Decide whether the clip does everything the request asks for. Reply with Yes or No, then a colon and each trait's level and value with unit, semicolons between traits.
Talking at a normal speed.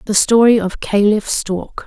Yes: average, 160 wpm